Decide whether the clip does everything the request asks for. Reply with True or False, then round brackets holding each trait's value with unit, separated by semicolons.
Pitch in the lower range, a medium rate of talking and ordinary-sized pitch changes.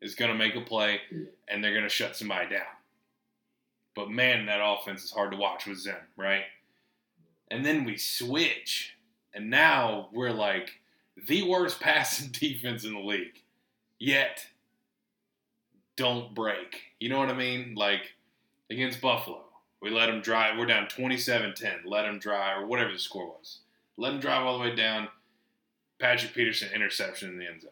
True (110 Hz; 175 wpm; 3.5 semitones)